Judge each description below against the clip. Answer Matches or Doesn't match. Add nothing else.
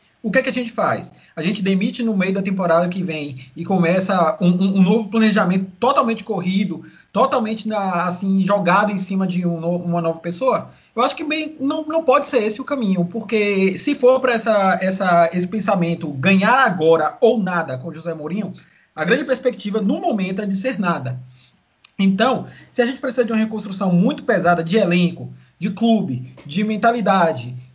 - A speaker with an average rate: Doesn't match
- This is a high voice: Matches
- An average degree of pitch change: Matches